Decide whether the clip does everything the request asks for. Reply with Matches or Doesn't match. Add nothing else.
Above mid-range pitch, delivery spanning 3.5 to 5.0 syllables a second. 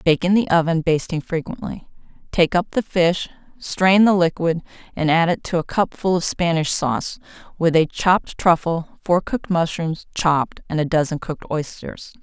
Doesn't match